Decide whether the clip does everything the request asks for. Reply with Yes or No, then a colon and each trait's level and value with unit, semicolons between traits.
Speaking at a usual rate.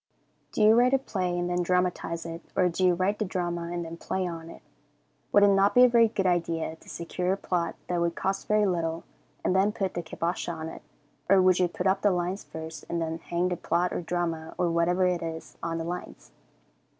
No: fast, 235 wpm